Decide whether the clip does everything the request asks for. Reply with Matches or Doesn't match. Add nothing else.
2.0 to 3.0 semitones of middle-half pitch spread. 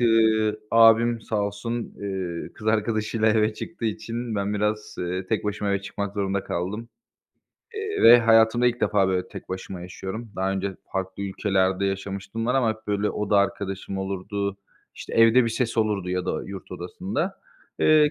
Matches